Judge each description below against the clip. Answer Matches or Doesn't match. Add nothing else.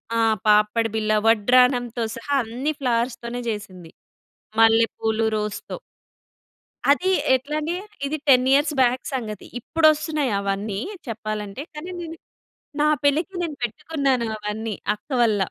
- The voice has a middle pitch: Doesn't match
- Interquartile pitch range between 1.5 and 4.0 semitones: Doesn't match